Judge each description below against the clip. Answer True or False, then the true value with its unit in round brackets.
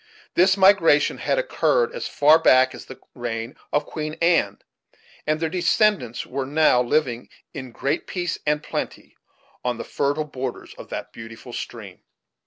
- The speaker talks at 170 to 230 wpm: False (155 wpm)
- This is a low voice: False (150 Hz)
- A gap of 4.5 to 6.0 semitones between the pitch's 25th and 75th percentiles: True (5.0 semitones)